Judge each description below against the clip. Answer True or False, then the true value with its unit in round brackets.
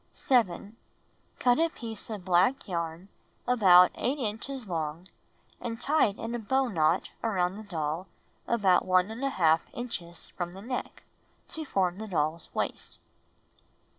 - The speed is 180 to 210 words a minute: False (135 wpm)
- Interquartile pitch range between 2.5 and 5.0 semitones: False (5.4 semitones)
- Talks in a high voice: True (200 Hz)